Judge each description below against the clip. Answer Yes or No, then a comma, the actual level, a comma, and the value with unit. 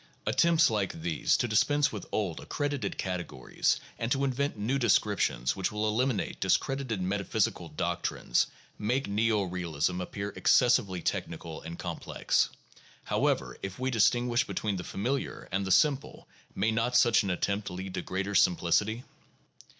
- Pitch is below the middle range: Yes, low, 105 Hz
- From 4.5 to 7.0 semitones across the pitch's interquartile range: Yes, average, 4.9 semitones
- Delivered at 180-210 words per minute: No, average, 145 wpm